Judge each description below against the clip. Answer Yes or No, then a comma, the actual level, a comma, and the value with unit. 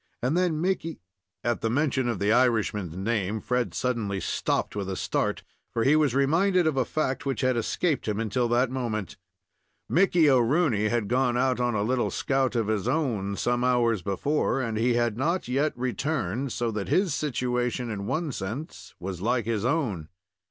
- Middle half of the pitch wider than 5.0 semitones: No, average, 4.1 semitones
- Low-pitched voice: Yes, low, 120 Hz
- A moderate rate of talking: Yes, average, 185 wpm